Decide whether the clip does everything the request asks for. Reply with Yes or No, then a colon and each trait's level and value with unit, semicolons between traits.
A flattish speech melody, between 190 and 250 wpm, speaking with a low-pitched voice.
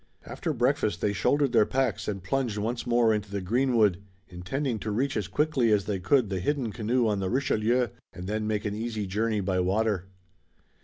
No: average, 3.5 semitones; average, 195 wpm; low, 110 Hz